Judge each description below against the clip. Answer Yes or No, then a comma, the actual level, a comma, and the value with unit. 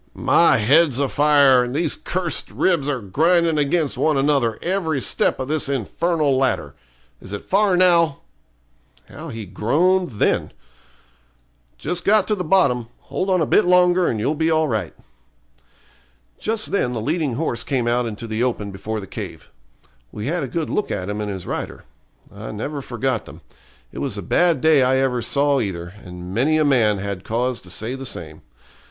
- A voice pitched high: No, low, 135 Hz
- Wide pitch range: Yes, wide, 6.4 semitones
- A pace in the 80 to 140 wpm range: No, average, 180 wpm